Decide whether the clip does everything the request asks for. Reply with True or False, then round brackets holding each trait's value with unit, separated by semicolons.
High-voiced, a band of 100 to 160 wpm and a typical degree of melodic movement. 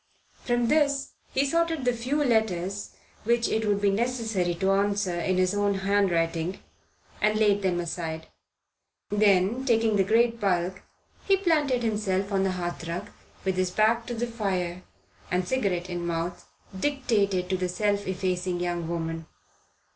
True (200 Hz; 150 wpm; 4.3 semitones)